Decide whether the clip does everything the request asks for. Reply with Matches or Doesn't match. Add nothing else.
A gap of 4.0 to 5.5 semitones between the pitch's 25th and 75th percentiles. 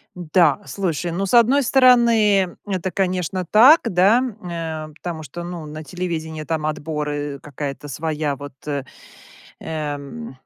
Matches